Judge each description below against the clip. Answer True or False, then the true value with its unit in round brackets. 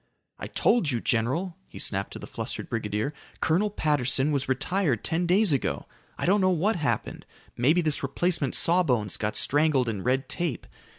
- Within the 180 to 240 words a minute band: False (170 wpm)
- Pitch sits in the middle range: True (145 Hz)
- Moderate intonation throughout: False (5.9 semitones)